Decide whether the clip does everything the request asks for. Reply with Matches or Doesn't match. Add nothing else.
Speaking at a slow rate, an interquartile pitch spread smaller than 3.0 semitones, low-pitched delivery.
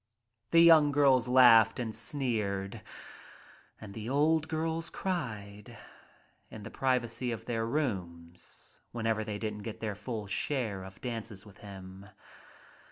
Doesn't match